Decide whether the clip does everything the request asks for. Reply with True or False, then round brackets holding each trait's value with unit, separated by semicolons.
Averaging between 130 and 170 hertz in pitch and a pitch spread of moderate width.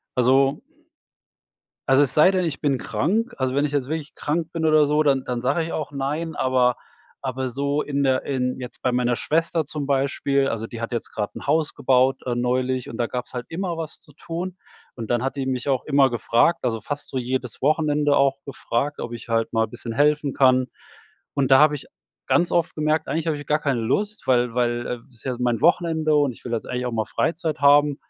True (135 Hz; 3.3 semitones)